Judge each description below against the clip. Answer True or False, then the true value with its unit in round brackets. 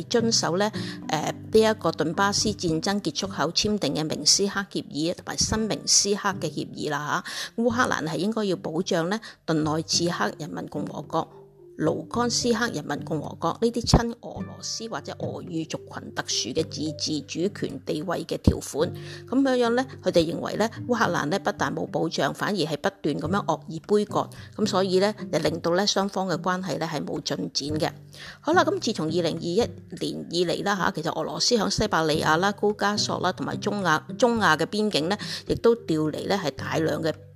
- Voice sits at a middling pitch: True (180 Hz)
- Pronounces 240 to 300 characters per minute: True (290 characters per minute)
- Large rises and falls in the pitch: False (4.9 semitones)